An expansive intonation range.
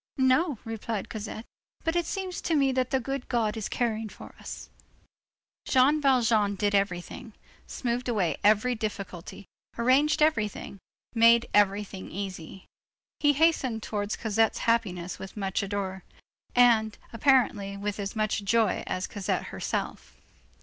No: average, 4.0 semitones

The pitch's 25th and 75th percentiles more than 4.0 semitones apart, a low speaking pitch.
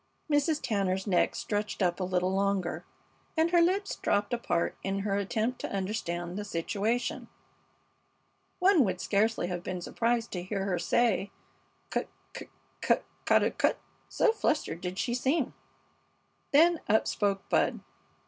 No: average, 4.6 semitones; high, 205 Hz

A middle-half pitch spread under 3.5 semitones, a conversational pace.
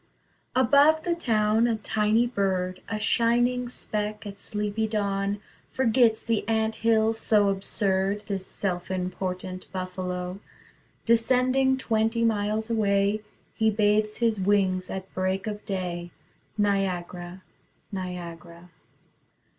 No: average, 3.1 semitones; slow, 110 wpm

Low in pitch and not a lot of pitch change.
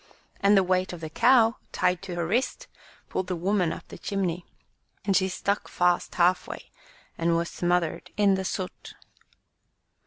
No: medium, 185 Hz; narrow, 2.2 semitones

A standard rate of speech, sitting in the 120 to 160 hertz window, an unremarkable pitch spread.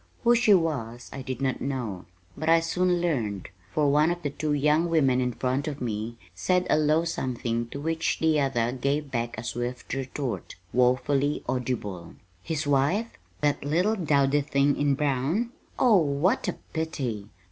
Yes: average, 170 wpm; medium, 140 Hz; average, 4.3 semitones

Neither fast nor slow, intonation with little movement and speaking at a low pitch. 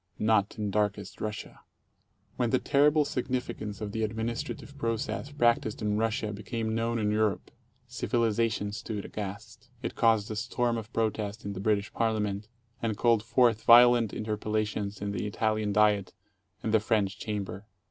Yes: average, 155 wpm; narrow, 1.8 semitones; low, 110 Hz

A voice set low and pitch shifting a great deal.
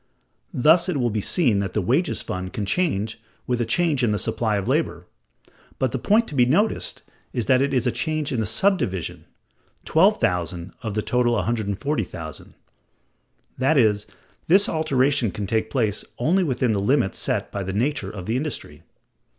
Yes: low, 120 Hz; wide, 6.3 semitones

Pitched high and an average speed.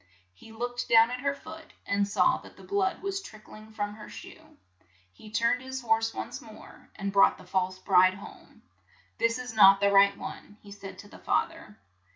No: high, 215 Hz; fast, 210 wpm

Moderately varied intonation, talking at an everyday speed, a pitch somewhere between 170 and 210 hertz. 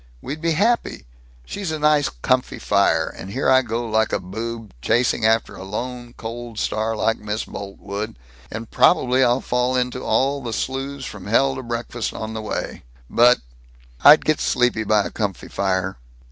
No: average, 3.4 semitones; average, 175 wpm; low, 120 Hz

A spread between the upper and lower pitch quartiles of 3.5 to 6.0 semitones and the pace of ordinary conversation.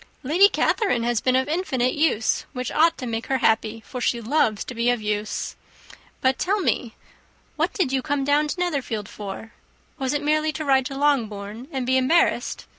Yes: average, 4.5 semitones; average, 190 wpm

